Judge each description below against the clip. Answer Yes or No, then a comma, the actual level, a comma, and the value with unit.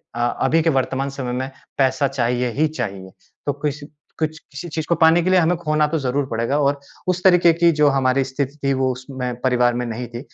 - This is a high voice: No, medium, 140 Hz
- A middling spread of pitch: Yes, average, 3.7 semitones